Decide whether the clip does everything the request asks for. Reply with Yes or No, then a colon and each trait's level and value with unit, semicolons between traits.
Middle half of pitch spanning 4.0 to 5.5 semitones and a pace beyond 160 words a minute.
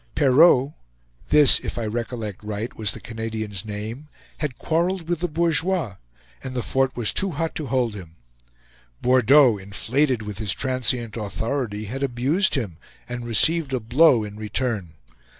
No: average, 5.1 semitones; average, 150 wpm